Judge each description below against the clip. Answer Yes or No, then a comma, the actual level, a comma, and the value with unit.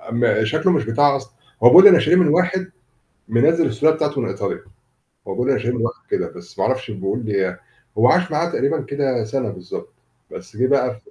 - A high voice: No, low, 135 Hz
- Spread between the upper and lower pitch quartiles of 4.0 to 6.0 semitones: Yes, wide, 5.4 semitones